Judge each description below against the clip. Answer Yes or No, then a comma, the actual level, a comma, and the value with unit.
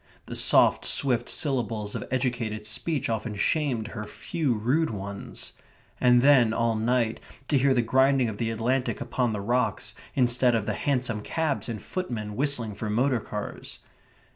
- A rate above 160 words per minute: No, average, 155 wpm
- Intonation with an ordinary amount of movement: Yes, average, 3.4 semitones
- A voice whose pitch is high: No, low, 120 Hz